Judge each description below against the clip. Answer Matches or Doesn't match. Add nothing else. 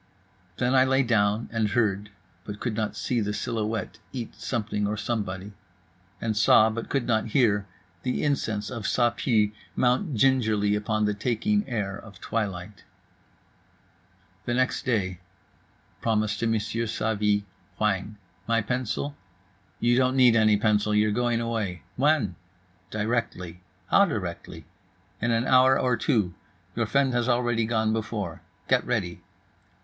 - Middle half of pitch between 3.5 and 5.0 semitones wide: Doesn't match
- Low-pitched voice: Matches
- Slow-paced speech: Matches